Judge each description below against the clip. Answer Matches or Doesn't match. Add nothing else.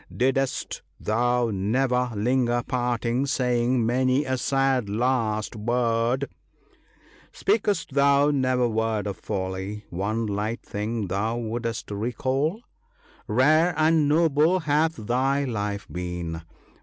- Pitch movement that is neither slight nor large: Matches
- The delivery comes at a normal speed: Doesn't match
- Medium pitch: Doesn't match